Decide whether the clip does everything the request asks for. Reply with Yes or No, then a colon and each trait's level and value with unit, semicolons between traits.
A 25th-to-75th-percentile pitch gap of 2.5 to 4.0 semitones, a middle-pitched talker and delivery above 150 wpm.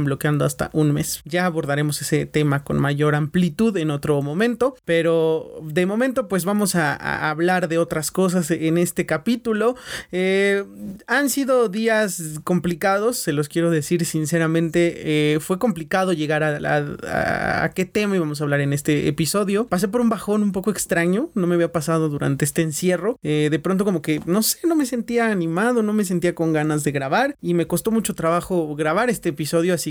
No: average, 4.7 semitones; medium, 175 Hz; fast, 190 wpm